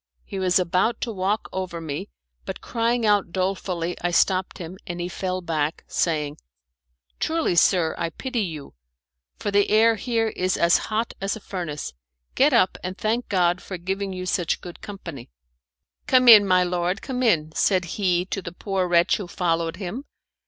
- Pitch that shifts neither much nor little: Yes, average, 3.1 semitones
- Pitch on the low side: No, medium, 185 Hz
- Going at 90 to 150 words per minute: No, average, 175 wpm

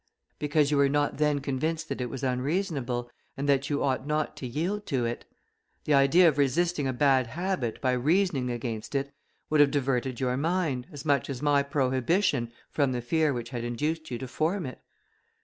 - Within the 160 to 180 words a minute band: No, average, 195 wpm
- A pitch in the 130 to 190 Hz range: Yes, medium, 140 Hz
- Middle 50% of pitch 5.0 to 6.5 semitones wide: No, average, 3.4 semitones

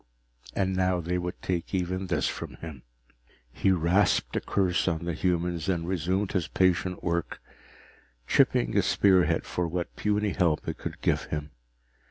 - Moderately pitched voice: No, very low, 90 Hz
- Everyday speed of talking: Yes, average, 160 wpm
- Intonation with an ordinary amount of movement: No, narrow, 1.8 semitones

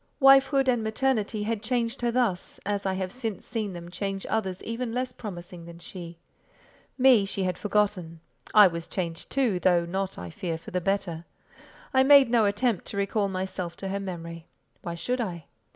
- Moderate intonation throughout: Yes, average, 4.7 semitones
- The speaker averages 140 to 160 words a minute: No, average, 185 wpm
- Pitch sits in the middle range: No, high, 200 Hz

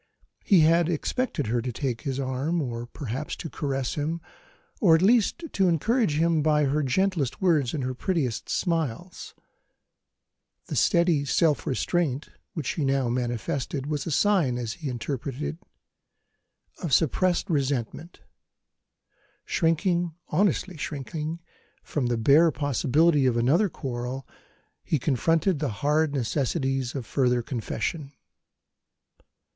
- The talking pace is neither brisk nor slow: No, slow, 130 wpm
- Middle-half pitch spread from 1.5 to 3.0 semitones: No, average, 4.5 semitones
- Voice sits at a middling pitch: Yes, medium, 145 Hz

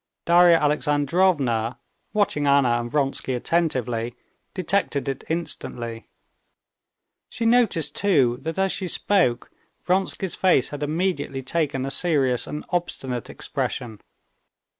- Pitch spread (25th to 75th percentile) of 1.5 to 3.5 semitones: No, wide, 5.6 semitones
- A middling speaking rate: No, slow, 110 wpm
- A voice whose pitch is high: No, medium, 150 Hz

